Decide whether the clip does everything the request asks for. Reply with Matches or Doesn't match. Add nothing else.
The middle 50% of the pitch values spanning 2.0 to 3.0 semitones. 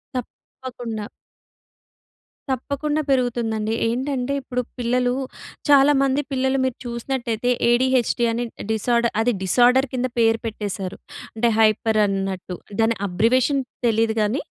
Matches